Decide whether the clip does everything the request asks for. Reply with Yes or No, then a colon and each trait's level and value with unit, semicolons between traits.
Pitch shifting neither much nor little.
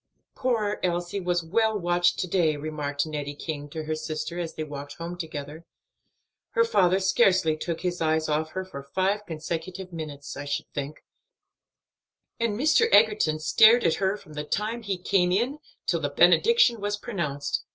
Yes: average, 4.7 semitones